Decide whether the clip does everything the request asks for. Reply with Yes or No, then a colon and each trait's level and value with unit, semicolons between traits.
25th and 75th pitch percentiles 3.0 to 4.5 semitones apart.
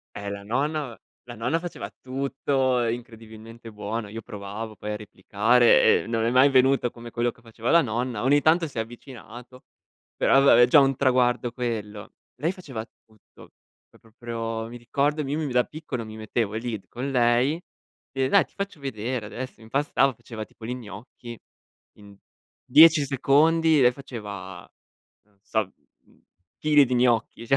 Yes: average, 3.4 semitones